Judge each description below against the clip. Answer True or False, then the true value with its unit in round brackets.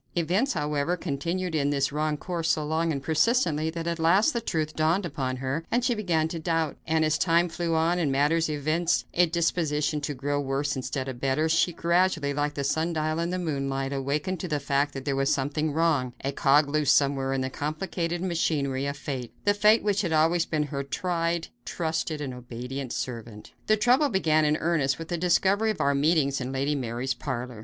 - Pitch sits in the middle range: True (155 Hz)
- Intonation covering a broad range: False (3.4 semitones)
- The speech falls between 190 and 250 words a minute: True (205 wpm)